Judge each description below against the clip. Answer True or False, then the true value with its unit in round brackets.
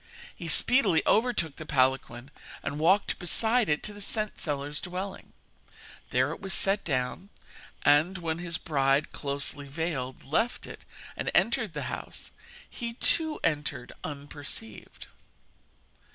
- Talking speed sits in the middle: False (130 wpm)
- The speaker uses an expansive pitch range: True (5.7 semitones)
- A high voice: False (160 Hz)